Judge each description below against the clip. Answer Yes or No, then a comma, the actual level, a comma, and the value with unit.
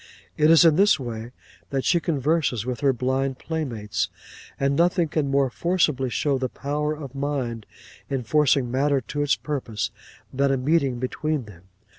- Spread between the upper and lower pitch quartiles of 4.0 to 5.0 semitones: No, average, 3.2 semitones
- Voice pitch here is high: No, low, 135 Hz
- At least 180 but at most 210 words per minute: No, average, 165 wpm